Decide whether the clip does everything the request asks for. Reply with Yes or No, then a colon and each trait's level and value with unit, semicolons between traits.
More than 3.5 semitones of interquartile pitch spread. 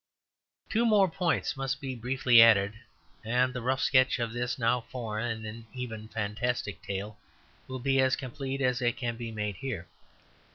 No: average, 2.9 semitones